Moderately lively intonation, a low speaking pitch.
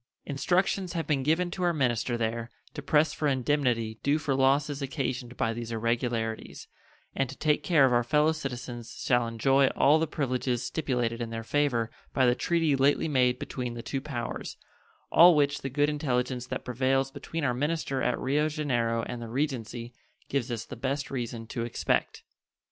Yes: average, 3.5 semitones; low, 130 Hz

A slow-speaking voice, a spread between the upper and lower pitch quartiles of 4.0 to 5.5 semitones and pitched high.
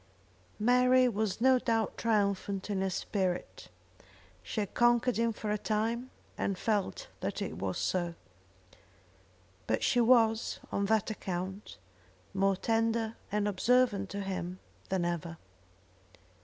No: slow, 130 wpm; average, 3.2 semitones; high, 210 Hz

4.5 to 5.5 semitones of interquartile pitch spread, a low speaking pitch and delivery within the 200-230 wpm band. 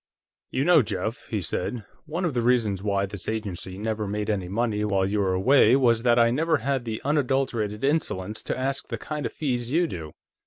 Yes: average, 4.8 semitones; low, 115 Hz; fast, 205 wpm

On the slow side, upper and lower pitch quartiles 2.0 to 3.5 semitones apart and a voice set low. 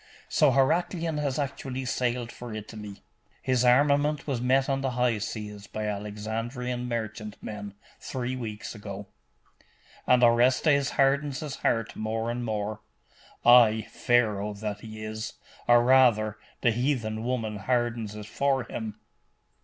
Yes: slow, 130 wpm; average, 3.1 semitones; low, 120 Hz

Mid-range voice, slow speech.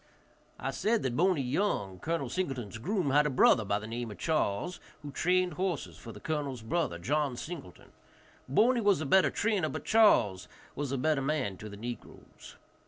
No: medium, 145 Hz; average, 180 wpm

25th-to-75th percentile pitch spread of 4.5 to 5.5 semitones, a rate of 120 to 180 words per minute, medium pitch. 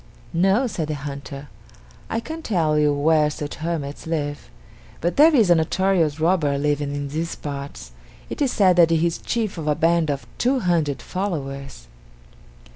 No: average, 3.9 semitones; average, 170 wpm; medium, 160 Hz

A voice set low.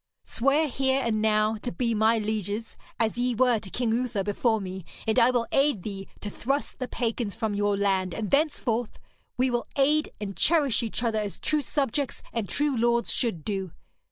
No: high, 230 Hz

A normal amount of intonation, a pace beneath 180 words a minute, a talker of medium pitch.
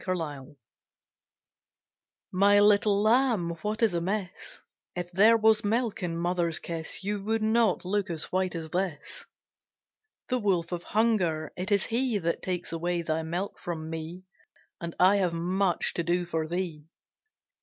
Yes: average, 3.6 semitones; average, 155 wpm; medium, 180 Hz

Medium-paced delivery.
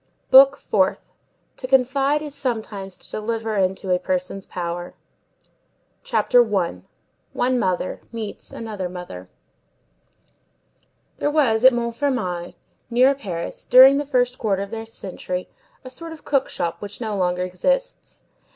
No: slow, 125 wpm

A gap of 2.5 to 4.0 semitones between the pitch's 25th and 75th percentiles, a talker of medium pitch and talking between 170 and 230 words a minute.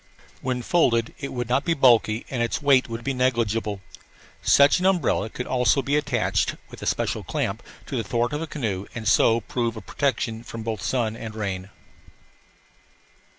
No: average, 3.4 semitones; low, 120 Hz; average, 180 wpm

